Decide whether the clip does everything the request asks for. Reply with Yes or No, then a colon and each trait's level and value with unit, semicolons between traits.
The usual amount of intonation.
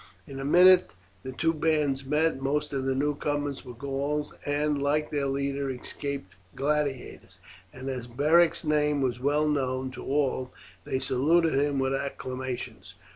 No: narrow, 2.1 semitones